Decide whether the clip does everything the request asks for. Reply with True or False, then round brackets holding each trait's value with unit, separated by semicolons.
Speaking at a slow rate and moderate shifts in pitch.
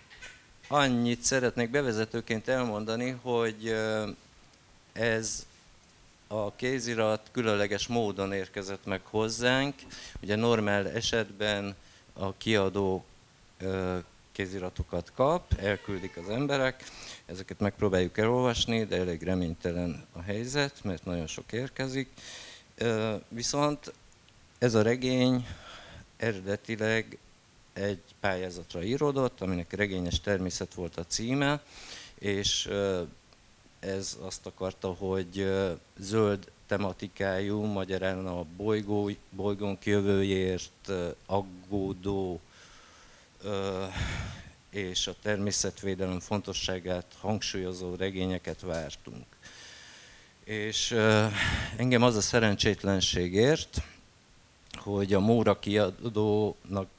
True (80 wpm; 3.1 semitones)